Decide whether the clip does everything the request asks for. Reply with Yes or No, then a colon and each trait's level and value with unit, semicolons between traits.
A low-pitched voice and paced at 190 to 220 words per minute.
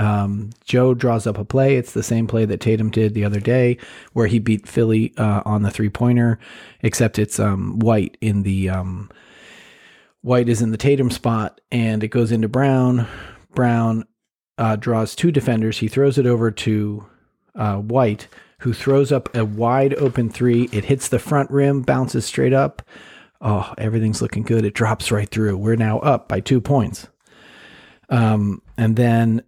No: low, 115 Hz; average, 175 wpm